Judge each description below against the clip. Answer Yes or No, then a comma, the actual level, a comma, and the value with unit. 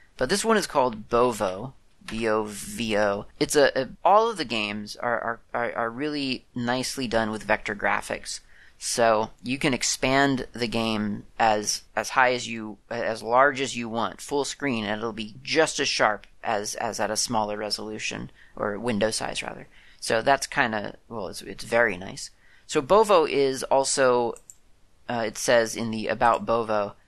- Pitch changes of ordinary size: Yes, average, 3.5 semitones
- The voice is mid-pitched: No, low, 115 Hz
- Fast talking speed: No, average, 170 wpm